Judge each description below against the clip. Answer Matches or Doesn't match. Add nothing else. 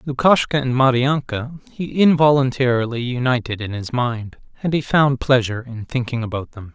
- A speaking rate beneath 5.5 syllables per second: Matches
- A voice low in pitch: Matches